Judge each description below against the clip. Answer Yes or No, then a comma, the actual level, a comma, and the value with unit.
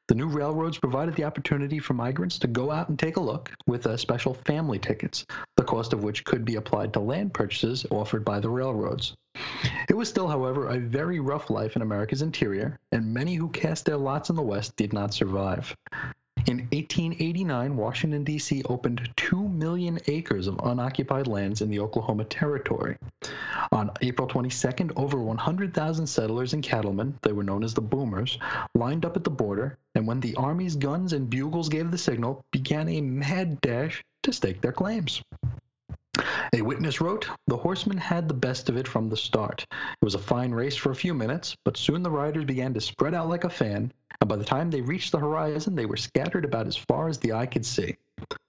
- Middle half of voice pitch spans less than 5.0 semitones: No, average, 5.3 semitones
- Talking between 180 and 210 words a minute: Yes, average, 200 wpm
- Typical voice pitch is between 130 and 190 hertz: Yes, medium, 140 Hz